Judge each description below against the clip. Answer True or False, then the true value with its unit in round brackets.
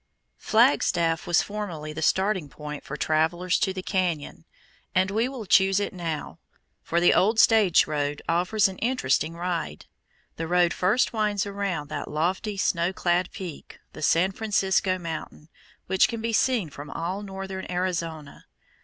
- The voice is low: False (185 Hz)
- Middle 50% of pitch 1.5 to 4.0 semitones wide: True (3.4 semitones)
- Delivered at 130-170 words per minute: True (155 wpm)